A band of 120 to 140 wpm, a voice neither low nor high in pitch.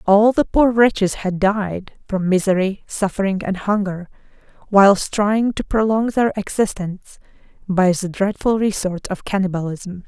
No: slow, 135 wpm; high, 200 Hz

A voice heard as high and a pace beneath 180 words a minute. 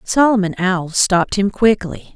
Yes: high, 195 Hz; average, 140 wpm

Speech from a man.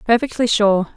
No: female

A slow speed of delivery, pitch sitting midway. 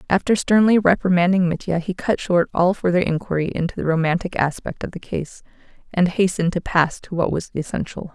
No: average, 185 wpm; medium, 180 Hz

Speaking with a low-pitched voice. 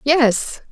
No: very high, 270 Hz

